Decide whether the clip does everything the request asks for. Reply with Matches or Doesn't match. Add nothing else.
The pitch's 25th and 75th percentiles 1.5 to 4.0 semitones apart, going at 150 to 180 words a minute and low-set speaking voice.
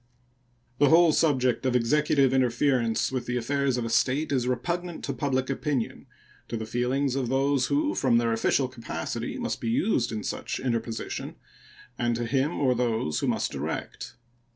Matches